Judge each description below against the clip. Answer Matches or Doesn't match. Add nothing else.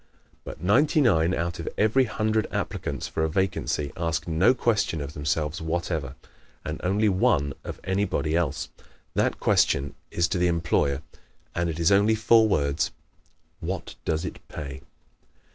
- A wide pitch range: Doesn't match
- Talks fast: Doesn't match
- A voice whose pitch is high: Doesn't match